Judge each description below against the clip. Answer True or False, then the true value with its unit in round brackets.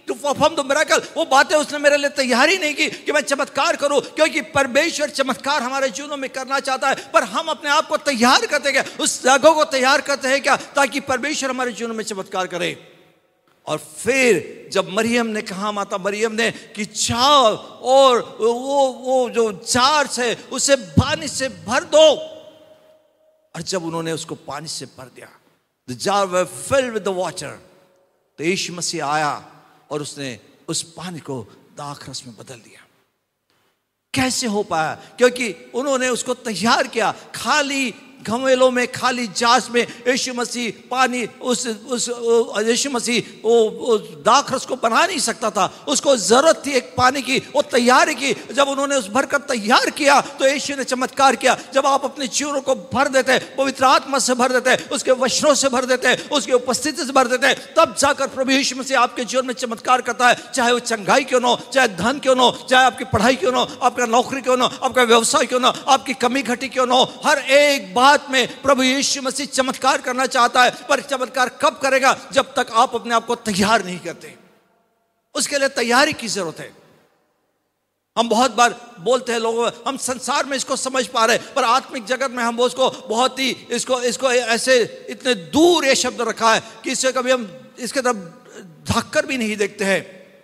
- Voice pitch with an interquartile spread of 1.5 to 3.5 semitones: True (3.1 semitones)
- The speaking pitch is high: True (255 Hz)